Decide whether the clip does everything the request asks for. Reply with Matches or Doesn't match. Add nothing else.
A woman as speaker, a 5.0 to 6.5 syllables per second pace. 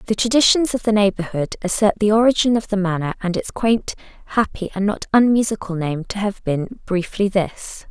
Matches